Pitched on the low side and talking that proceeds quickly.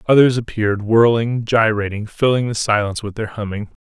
No: low, 110 Hz; average, 155 wpm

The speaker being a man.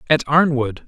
Yes: male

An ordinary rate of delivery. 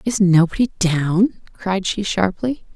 No: slow, 130 wpm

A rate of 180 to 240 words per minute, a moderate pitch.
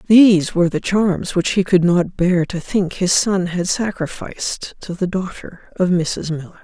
Yes: average, 190 wpm; medium, 180 Hz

